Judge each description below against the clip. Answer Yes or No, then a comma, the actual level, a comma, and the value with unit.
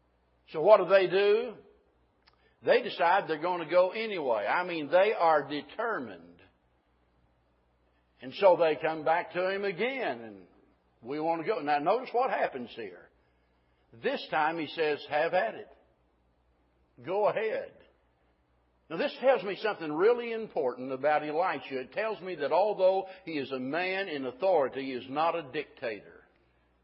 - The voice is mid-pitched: Yes, medium, 150 Hz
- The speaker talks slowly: No, average, 155 wpm